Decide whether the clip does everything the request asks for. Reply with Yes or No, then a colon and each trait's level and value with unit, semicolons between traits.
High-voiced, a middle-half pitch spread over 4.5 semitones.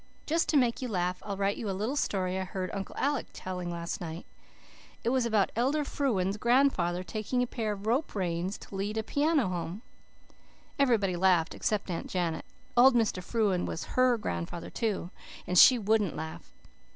Yes: high, 205 Hz; average, 4.9 semitones